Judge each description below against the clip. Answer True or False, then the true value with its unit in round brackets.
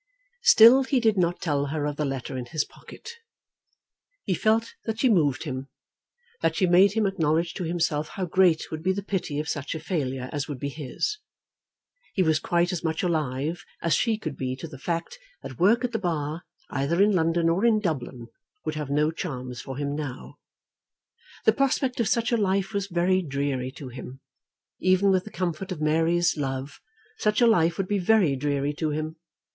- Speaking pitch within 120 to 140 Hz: False (165 Hz)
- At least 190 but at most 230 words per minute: True (195 wpm)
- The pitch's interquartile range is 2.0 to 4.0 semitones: False (5.1 semitones)